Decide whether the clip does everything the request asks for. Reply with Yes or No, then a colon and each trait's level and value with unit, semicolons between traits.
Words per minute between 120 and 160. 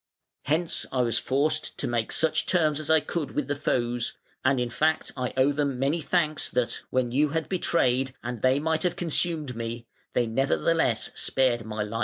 No: average, 190 wpm